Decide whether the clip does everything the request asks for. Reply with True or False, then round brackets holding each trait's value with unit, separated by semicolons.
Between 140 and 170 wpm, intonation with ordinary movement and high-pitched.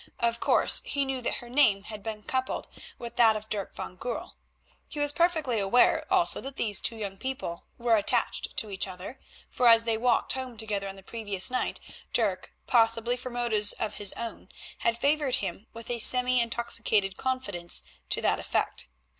False (185 wpm; 3.3 semitones; 230 Hz)